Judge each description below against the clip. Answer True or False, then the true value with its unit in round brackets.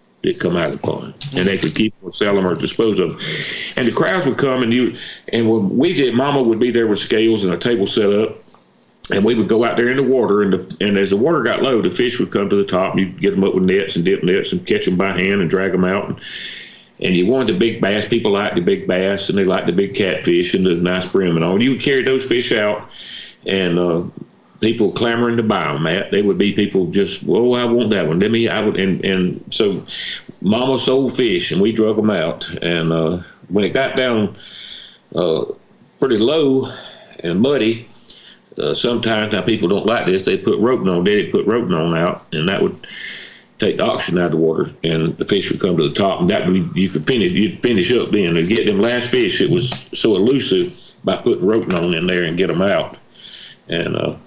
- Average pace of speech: False (250 wpm)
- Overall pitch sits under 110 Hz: True (100 Hz)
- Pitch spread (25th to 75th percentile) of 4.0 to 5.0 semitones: True (4.4 semitones)